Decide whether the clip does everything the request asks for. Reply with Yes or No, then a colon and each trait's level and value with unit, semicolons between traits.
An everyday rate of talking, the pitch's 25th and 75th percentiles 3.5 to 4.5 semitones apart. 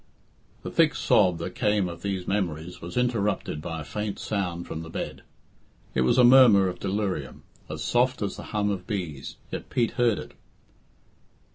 Yes: average, 175 wpm; average, 3.8 semitones